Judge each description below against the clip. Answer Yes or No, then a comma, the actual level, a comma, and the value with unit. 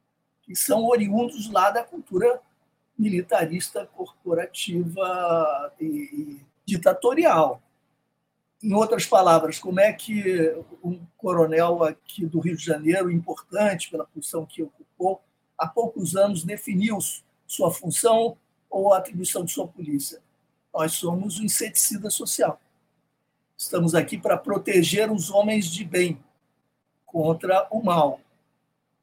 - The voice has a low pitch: No, medium, 180 Hz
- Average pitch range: Yes, average, 4.4 semitones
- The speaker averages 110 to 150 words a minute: Yes, slow, 120 wpm